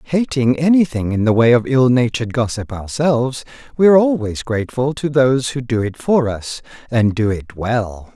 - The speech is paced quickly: No, average, 185 wpm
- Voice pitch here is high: No, low, 125 Hz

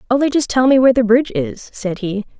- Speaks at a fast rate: Yes, fast, 250 wpm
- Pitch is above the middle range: Yes, high, 235 Hz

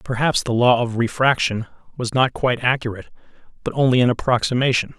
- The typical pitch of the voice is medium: No, low, 125 Hz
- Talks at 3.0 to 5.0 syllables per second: No, 6.2 syllables/s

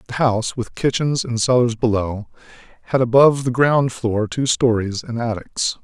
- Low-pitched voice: Yes, low, 120 Hz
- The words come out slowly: No, average, 165 wpm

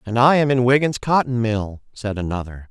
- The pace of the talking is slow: No, average, 200 wpm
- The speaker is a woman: No, male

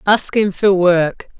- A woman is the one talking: Yes, female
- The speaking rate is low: Yes, slow, 130 wpm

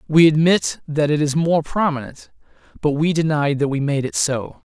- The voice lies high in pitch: No, medium, 150 Hz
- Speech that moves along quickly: No, average, 190 wpm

